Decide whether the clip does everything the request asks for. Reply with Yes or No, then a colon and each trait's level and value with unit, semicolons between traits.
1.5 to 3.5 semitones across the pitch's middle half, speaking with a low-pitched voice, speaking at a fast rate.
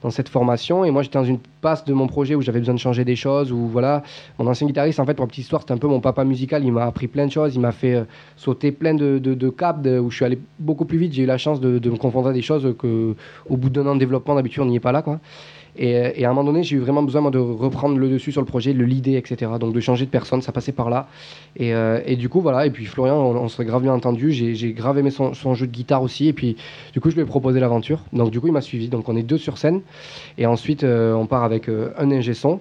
Yes: average, 2.8 semitones; low, 130 Hz; fast, 315 wpm